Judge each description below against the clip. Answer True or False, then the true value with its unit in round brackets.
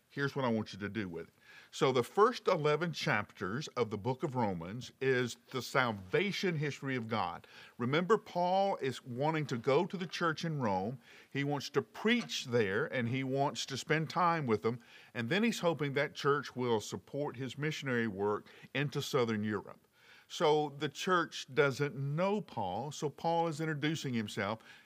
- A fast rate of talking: False (180 wpm)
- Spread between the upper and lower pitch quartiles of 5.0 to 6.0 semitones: True (5.3 semitones)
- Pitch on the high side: False (140 Hz)